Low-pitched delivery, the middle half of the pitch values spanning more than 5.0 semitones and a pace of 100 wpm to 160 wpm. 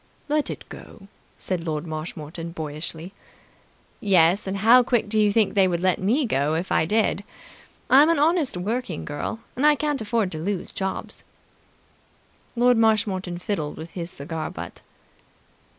No: high, 190 Hz; wide, 5.6 semitones; average, 155 wpm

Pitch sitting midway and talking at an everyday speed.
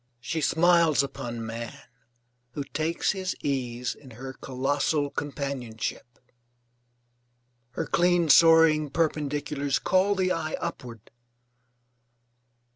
No: medium, 145 Hz; slow, 95 wpm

